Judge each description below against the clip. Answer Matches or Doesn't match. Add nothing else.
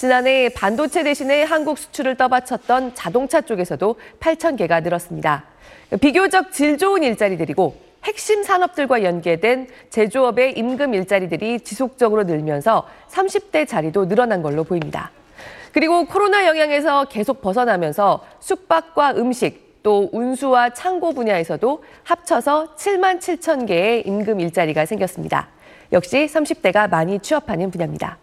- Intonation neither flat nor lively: Doesn't match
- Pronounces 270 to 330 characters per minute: Matches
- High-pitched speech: Matches